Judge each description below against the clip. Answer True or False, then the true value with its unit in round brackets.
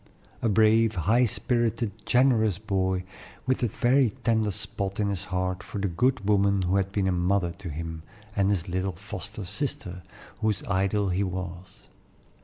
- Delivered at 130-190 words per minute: True (165 wpm)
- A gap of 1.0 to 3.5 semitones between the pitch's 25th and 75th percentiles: True (3.1 semitones)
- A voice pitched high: False (100 Hz)